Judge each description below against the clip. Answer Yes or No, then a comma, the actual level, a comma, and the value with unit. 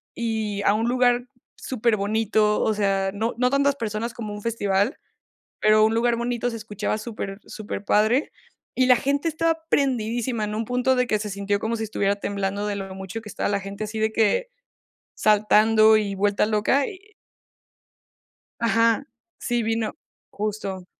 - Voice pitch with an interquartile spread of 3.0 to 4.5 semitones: No, narrow, 2.5 semitones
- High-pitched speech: Yes, high, 220 Hz